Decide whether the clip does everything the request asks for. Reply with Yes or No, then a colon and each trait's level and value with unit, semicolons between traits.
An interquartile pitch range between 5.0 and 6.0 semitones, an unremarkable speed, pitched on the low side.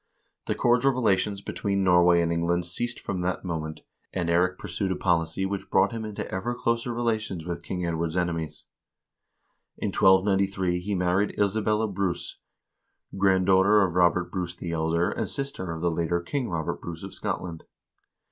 No: average, 2.7 semitones; average, 165 wpm; very low, 90 Hz